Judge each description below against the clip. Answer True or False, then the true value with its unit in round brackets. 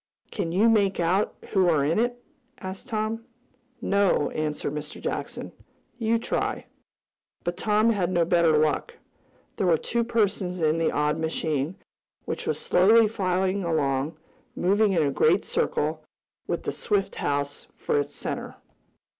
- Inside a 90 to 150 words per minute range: True (145 wpm)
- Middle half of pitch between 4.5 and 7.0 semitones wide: True (5.2 semitones)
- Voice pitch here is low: False (180 Hz)